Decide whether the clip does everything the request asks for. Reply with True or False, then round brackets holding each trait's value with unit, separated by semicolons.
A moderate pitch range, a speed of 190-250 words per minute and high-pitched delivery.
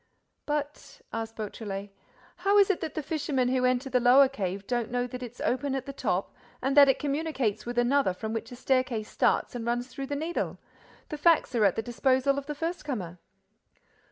True (3.8 semitones; 205 wpm; 255 Hz)